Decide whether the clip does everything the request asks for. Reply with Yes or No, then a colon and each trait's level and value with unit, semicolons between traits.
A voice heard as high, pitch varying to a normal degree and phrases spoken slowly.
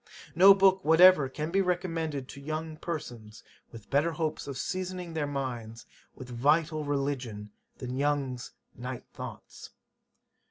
No: medium, 145 Hz; average, 4.5 semitones; slow, 130 wpm